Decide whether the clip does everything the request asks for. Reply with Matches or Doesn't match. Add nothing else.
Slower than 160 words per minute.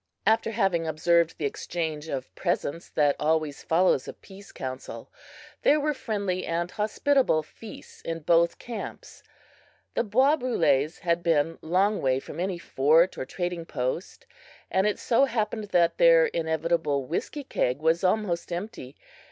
Matches